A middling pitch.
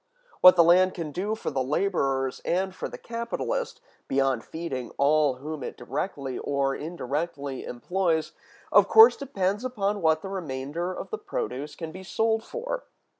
Yes: medium, 170 Hz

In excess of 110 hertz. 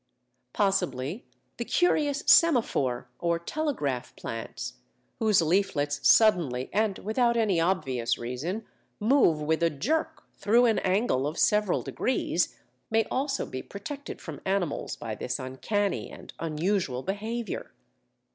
Yes: high, 190 Hz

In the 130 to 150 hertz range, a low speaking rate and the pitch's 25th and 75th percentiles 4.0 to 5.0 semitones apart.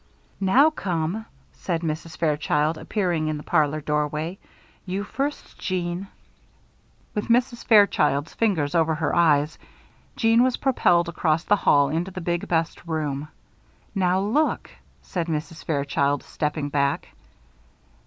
No: medium, 165 Hz; slow, 125 wpm; average, 4.3 semitones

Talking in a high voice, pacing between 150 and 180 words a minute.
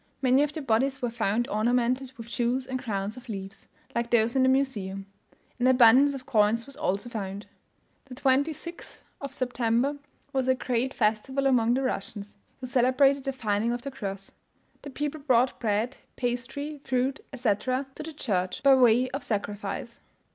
Yes: very high, 250 Hz; average, 170 wpm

